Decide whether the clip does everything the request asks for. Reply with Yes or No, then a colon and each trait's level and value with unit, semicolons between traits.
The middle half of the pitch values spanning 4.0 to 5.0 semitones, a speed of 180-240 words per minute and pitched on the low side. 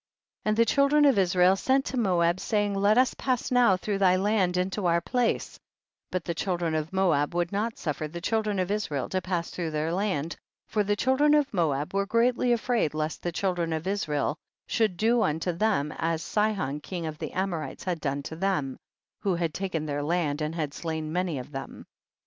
No: average, 4.7 semitones; fast, 205 wpm; medium, 180 Hz